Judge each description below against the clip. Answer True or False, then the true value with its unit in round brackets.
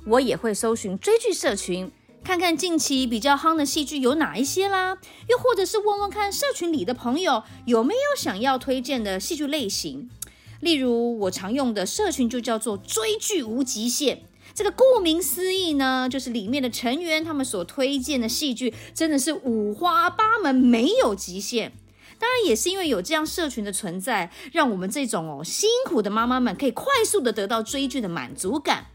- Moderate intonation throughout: False (6.5 semitones)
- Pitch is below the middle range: False (275 Hz)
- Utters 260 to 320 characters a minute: True (285 characters per minute)